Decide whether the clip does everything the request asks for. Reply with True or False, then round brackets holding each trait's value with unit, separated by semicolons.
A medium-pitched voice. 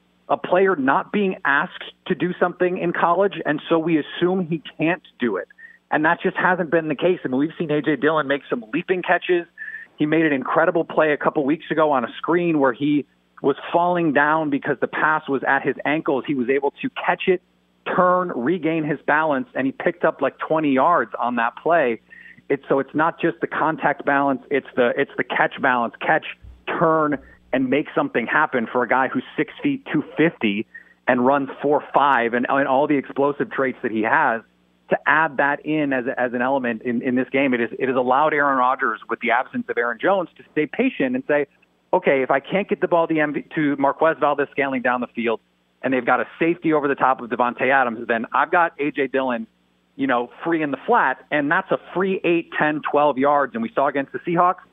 True (150 Hz)